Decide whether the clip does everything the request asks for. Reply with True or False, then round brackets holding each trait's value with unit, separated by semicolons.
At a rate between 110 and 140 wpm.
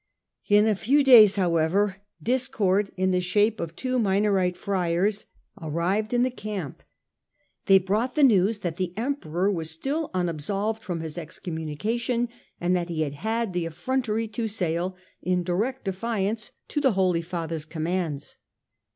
False (150 wpm)